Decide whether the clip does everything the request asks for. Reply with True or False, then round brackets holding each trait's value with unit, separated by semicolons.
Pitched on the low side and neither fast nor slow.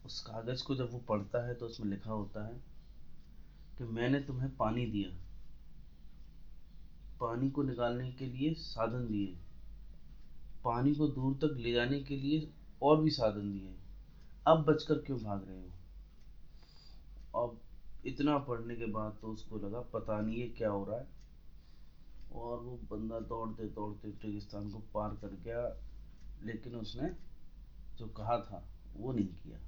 True (110 Hz; 150 wpm)